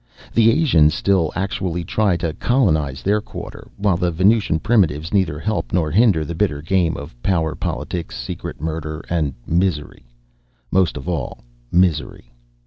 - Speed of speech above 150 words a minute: No, average, 145 wpm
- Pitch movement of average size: Yes, average, 4.1 semitones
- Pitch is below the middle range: Yes, very low, 85 Hz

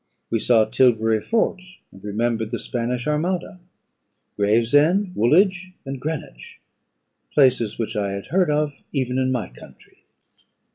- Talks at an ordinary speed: No, slow, 130 wpm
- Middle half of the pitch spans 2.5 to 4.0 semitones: No, wide, 5.4 semitones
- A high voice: No, low, 125 Hz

